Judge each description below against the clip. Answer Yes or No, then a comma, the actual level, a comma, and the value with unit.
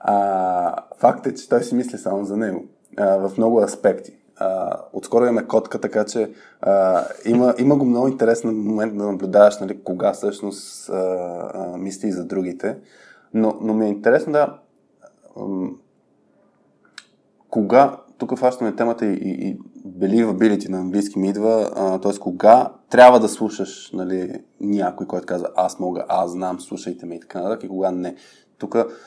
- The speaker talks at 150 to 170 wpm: Yes, fast, 165 wpm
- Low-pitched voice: Yes, low, 105 Hz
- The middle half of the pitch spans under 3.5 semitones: Yes, average, 2.9 semitones